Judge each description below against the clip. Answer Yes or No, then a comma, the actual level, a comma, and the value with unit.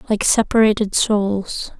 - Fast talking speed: No, slow, 100 wpm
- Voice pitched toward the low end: No, high, 210 Hz